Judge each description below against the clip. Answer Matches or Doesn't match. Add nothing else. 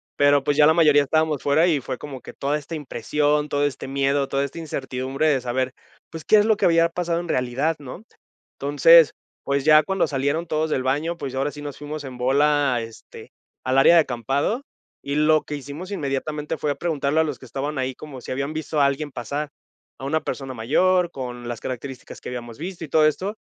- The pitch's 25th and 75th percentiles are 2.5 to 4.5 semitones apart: Matches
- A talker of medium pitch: Matches